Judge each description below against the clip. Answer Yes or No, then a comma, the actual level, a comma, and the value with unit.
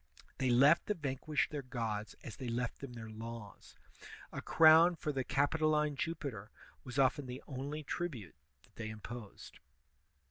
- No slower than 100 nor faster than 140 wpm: No, average, 150 wpm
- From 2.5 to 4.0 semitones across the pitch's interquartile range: No, average, 4.5 semitones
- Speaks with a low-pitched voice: Yes, low, 130 Hz